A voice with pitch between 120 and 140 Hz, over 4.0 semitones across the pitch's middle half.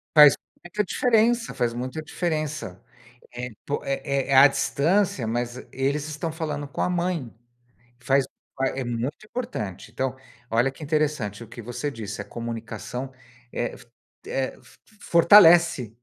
Yes: low, 135 Hz; average, 4.9 semitones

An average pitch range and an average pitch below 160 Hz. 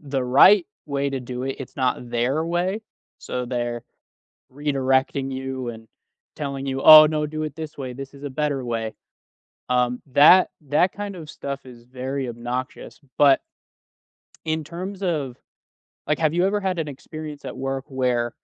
Yes: average, 3.4 semitones; low, 135 Hz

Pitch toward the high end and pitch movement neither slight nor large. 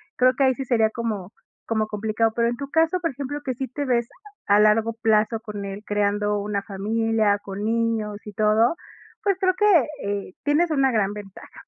Yes: high, 225 Hz; average, 3.9 semitones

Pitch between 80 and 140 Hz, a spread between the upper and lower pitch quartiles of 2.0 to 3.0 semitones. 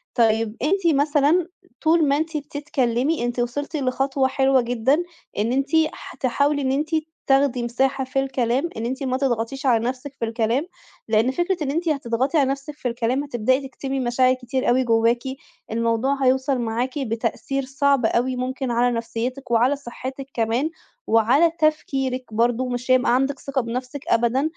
No: very high, 260 Hz; average, 2.7 semitones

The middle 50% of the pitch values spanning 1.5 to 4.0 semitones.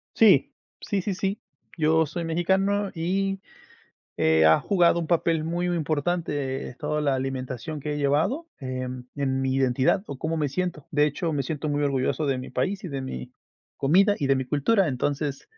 No: average, 4.6 semitones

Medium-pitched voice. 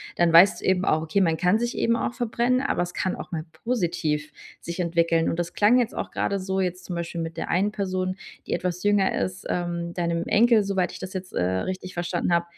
Yes: medium, 180 Hz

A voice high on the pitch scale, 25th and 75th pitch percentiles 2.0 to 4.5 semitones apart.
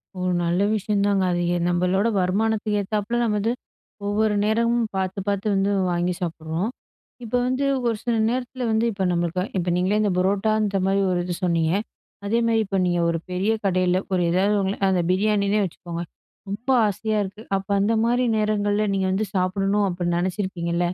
Yes: high, 200 Hz; average, 2.8 semitones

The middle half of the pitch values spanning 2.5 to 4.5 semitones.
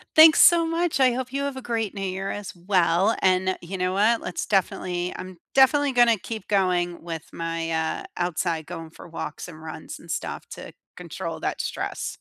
No: wide, 5.6 semitones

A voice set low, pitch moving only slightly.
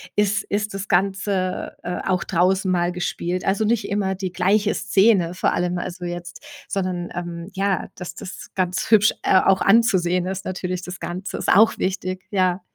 No: medium, 185 Hz; narrow, 1.9 semitones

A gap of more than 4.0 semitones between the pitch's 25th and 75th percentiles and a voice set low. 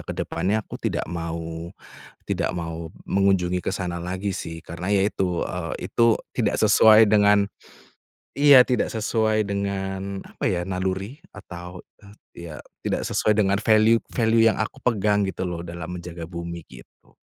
No: average, 3.5 semitones; very low, 95 Hz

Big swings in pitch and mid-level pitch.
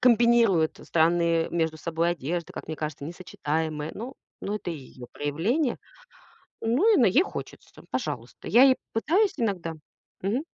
Yes: wide, 6.8 semitones; medium, 175 Hz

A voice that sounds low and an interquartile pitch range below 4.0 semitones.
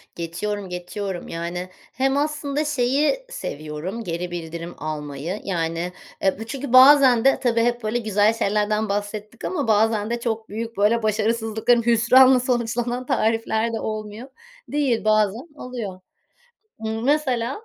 No: high, 225 Hz; average, 3.6 semitones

